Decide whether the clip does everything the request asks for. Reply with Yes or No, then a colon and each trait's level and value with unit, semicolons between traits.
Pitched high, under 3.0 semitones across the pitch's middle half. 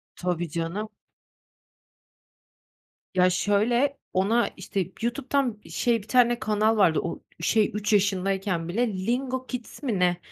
No: high, 210 Hz; average, 4.6 semitones